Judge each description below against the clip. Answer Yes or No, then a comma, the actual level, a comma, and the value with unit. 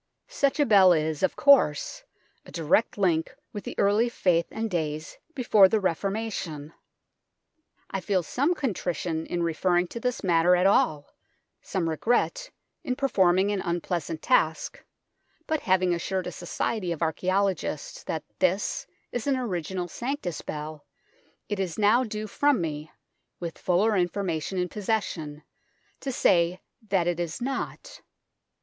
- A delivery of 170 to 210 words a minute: No, average, 145 wpm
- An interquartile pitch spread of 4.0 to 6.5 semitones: Yes, average, 4.9 semitones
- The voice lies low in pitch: No, medium, 185 Hz